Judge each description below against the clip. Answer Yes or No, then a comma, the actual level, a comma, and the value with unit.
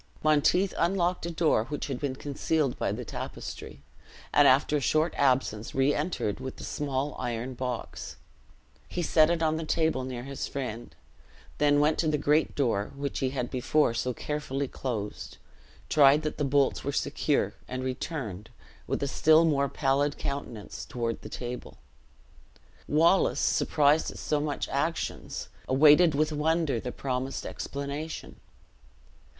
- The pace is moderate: Yes, average, 150 wpm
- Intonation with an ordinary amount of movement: Yes, average, 3.0 semitones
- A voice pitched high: No, medium, 140 Hz